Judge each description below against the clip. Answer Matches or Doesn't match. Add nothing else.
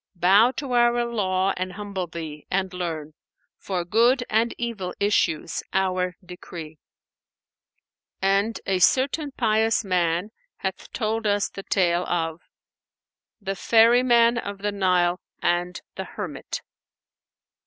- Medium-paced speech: Doesn't match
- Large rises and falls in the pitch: Doesn't match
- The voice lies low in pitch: Doesn't match